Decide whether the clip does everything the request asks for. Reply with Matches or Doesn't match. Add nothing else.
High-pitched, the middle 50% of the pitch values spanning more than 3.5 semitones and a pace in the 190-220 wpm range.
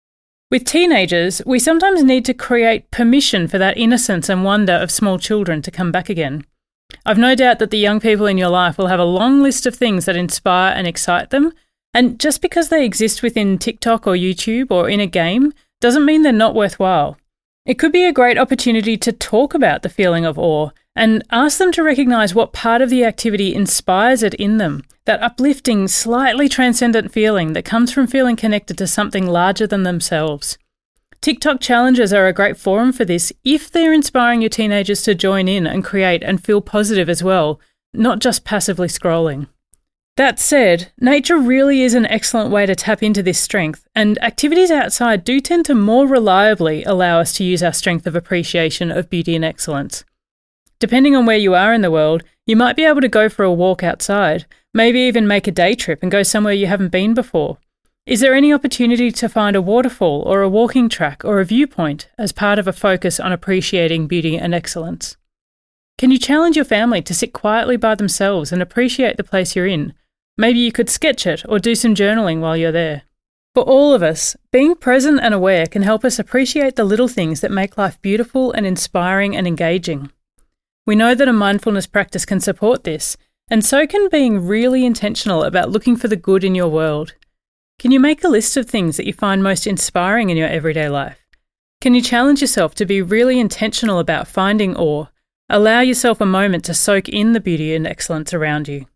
Matches